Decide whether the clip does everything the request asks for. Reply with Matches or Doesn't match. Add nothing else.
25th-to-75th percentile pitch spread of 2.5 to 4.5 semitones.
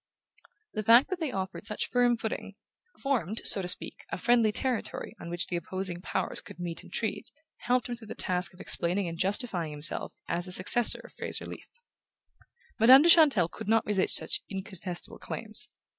Doesn't match